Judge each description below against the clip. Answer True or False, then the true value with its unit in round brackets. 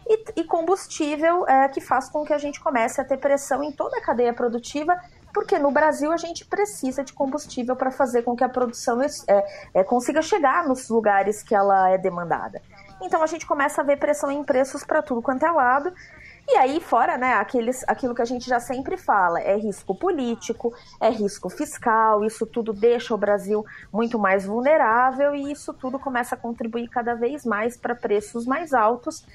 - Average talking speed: False (195 wpm)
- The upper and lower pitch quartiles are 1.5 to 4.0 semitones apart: False (4.5 semitones)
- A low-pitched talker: False (255 Hz)